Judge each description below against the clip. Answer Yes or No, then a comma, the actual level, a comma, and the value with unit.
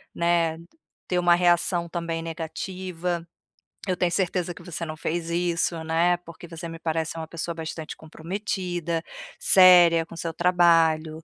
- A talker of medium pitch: Yes, medium, 170 Hz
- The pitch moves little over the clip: Yes, narrow, 1.4 semitones